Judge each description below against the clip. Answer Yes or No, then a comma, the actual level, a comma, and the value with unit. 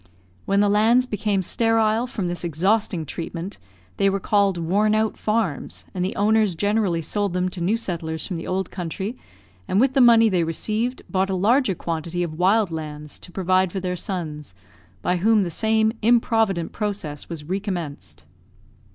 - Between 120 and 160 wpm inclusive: No, average, 170 wpm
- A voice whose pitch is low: No, high, 190 Hz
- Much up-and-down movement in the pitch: No, average, 4.1 semitones